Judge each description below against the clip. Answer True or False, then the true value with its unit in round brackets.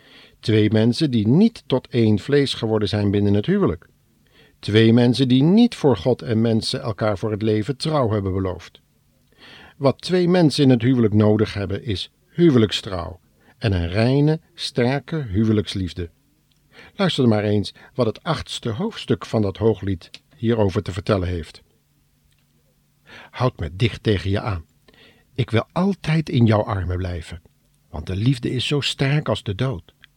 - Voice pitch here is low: True (110 Hz)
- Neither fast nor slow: True (155 wpm)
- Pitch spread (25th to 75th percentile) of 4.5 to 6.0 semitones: True (4.8 semitones)